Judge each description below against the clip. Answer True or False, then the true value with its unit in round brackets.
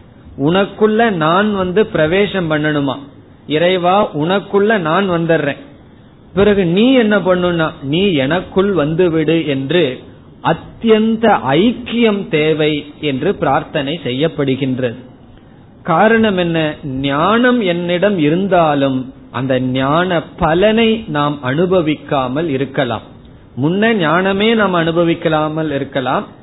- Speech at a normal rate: True (85 wpm)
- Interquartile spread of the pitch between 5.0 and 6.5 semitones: True (5.6 semitones)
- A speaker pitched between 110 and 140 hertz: False (160 Hz)